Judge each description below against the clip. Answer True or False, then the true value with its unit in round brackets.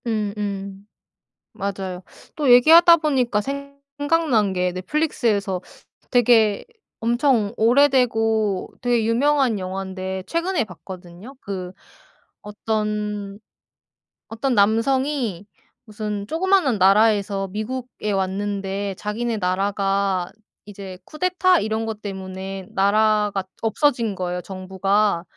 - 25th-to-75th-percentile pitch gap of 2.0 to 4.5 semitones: True (4.1 semitones)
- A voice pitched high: True (210 Hz)